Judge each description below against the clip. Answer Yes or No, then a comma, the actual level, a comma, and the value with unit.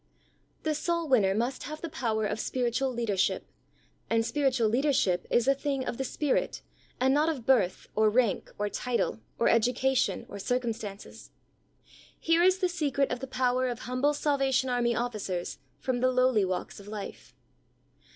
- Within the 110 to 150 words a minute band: No, average, 170 wpm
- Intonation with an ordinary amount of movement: Yes, average, 3.4 semitones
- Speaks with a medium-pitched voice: No, very high, 250 Hz